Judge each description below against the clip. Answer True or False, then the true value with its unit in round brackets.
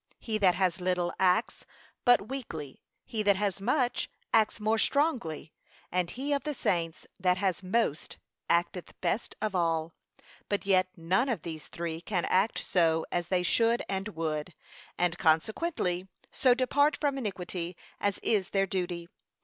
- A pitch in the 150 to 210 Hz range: True (185 Hz)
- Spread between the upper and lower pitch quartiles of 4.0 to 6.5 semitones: True (4.6 semitones)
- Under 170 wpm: True (155 wpm)